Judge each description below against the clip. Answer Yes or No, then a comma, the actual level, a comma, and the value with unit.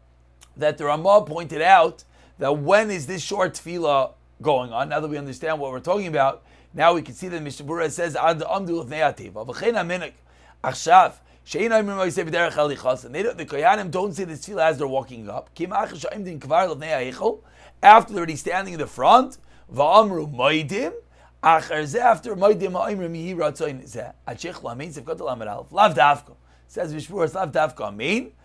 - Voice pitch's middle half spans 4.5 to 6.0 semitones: Yes, wide, 5.5 semitones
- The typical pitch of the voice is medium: Yes, medium, 160 Hz